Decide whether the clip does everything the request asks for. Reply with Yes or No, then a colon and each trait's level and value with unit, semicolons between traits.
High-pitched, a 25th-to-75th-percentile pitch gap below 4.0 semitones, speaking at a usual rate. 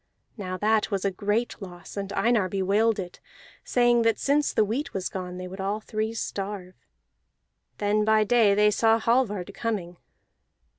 Yes: high, 210 Hz; average, 2.7 semitones; average, 160 wpm